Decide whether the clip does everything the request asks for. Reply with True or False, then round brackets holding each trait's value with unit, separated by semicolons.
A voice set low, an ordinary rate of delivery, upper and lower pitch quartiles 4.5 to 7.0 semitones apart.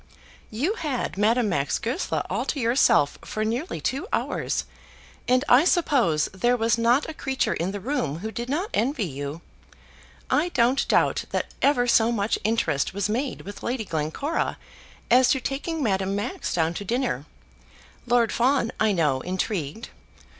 False (230 Hz; 160 wpm; 5.5 semitones)